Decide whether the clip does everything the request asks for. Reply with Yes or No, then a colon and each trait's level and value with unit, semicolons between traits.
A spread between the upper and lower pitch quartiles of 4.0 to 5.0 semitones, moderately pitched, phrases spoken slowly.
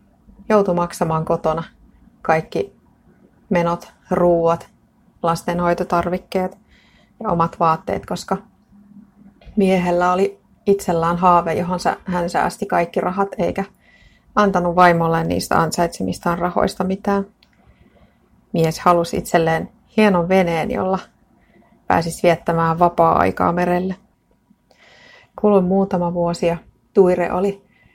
No: narrow, 2.4 semitones; medium, 180 Hz; slow, 90 wpm